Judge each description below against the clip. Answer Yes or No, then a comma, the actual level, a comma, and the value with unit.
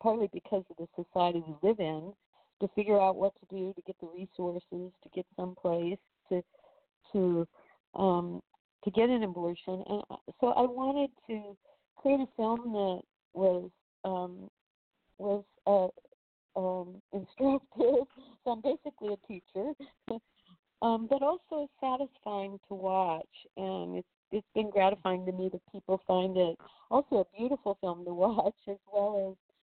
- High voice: Yes, high, 200 Hz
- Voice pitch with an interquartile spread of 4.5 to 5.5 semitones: No, average, 4.0 semitones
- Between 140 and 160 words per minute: Yes, average, 150 wpm